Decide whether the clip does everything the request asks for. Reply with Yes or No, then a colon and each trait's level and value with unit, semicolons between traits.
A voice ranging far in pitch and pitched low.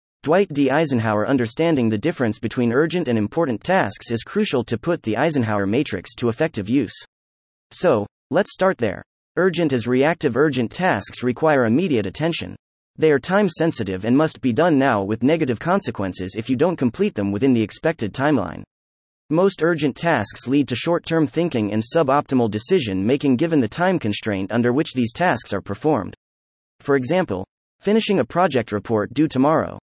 Yes: wide, 7.0 semitones; low, 130 Hz